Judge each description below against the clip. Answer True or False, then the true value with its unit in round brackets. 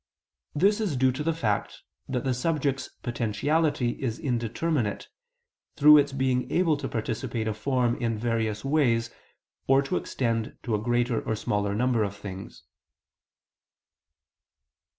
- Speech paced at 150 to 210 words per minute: False (140 wpm)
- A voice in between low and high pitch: False (125 Hz)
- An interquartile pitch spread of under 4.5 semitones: True (3.9 semitones)